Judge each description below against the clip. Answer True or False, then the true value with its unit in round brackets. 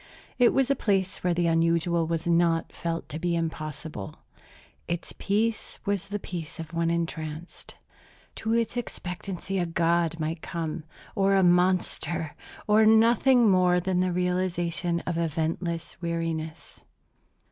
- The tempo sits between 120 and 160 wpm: True (135 wpm)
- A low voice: False (175 Hz)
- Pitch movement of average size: False (2.3 semitones)